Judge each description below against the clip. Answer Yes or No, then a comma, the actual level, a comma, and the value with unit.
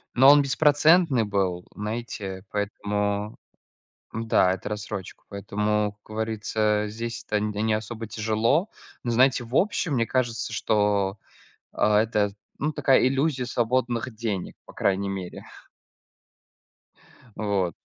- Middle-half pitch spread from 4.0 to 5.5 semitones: No, average, 2.9 semitones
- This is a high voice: No, low, 110 Hz